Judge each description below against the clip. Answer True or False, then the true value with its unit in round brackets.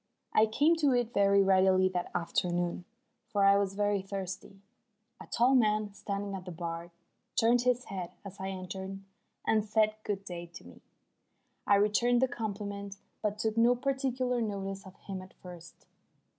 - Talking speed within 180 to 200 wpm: False (165 wpm)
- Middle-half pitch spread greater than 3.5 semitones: False (2.8 semitones)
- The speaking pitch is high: True (200 Hz)